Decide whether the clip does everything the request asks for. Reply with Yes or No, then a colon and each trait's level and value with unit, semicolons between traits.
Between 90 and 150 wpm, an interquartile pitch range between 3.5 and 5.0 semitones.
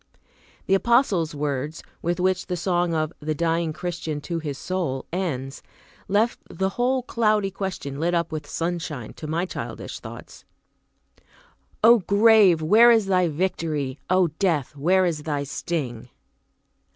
Yes: average, 140 wpm; average, 3.9 semitones